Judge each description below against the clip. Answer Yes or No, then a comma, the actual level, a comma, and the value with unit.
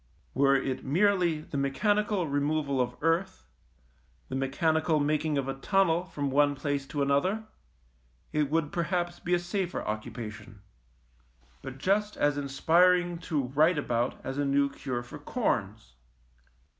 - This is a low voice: No, medium, 145 Hz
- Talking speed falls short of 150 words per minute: Yes, average, 140 wpm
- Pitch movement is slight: No, average, 4.1 semitones